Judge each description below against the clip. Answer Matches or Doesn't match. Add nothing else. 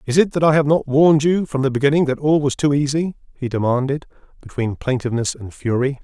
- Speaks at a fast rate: Matches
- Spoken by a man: Matches